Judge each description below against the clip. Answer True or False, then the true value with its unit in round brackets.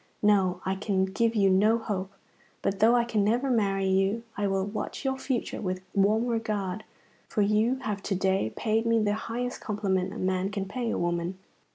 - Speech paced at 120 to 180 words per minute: False (195 wpm)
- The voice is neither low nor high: False (205 Hz)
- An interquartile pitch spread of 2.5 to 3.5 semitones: True (2.9 semitones)